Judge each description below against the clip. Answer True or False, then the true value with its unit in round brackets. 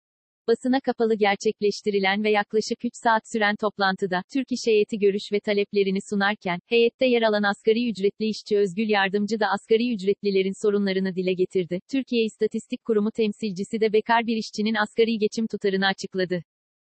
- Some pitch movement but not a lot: False (2.2 semitones)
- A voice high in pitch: True (210 Hz)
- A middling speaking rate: False (150 wpm)